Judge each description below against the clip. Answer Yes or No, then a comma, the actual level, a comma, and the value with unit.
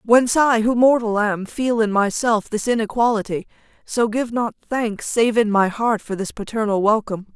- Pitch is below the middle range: No, high, 220 Hz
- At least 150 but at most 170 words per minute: No, average, 180 wpm